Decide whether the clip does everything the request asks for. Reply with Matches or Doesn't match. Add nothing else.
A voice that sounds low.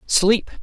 Doesn't match